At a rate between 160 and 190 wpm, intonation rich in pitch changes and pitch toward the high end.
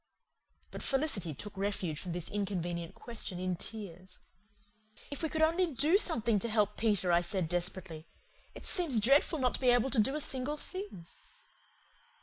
Yes: average, 165 wpm; wide, 7.2 semitones; high, 210 Hz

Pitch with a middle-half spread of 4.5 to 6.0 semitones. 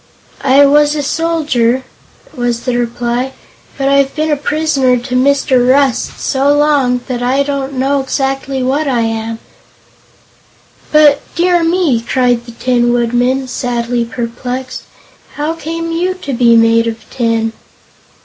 No: average, 2.9 semitones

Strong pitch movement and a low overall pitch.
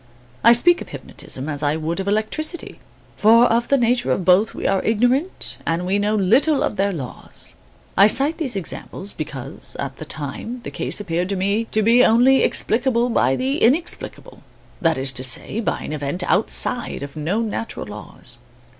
No: wide, 7.0 semitones; high, 205 Hz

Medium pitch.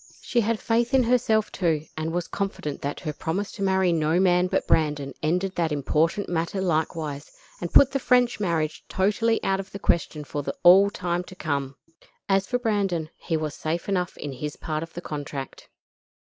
Yes: medium, 175 Hz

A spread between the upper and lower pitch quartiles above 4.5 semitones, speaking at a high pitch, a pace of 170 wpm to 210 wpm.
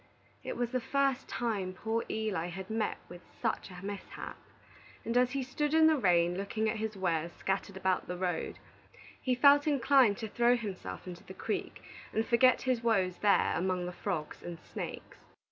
Yes: average, 5.0 semitones; high, 215 Hz; average, 180 wpm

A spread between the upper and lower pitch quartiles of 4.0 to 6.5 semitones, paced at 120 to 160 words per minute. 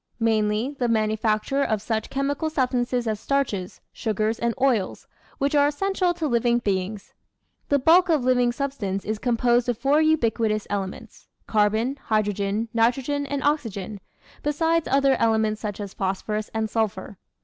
Yes: average, 4.5 semitones; average, 150 wpm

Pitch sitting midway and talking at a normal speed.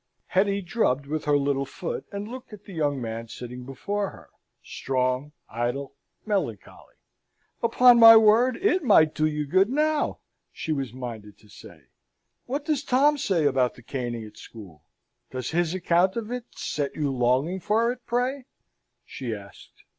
Yes: medium, 155 Hz; average, 160 wpm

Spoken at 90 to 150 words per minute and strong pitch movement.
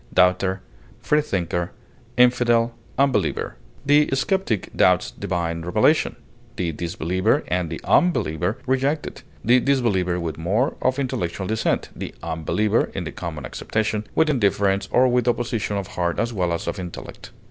Yes: slow, 135 wpm; wide, 5.9 semitones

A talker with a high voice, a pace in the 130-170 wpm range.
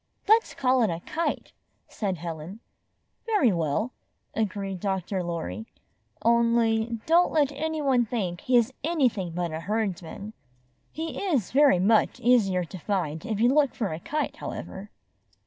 Yes: high, 220 Hz; average, 150 wpm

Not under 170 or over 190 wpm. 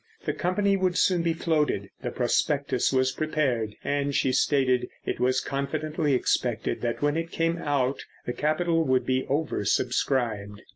No: average, 155 wpm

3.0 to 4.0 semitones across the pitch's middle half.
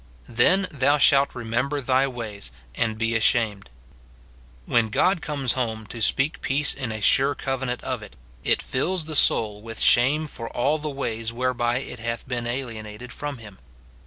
Yes: average, 3.4 semitones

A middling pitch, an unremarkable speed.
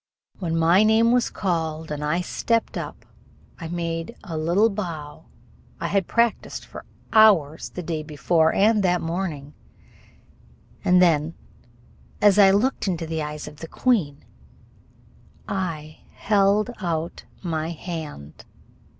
No: medium, 170 Hz; slow, 130 wpm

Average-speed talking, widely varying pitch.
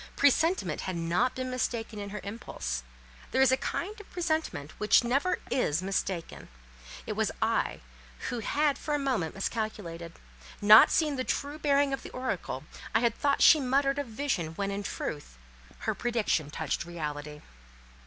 Yes: average, 165 wpm; wide, 8.2 semitones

